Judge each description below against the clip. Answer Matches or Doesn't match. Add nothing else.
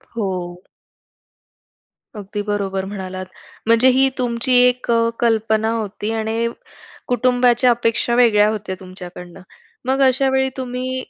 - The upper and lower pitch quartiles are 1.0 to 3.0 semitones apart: Doesn't match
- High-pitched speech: Matches